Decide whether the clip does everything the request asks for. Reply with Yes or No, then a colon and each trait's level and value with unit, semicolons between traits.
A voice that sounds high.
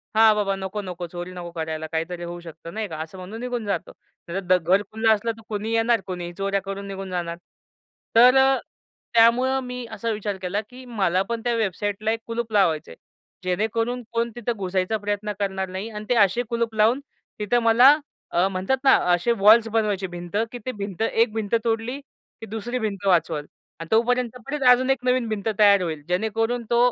Yes: high, 210 Hz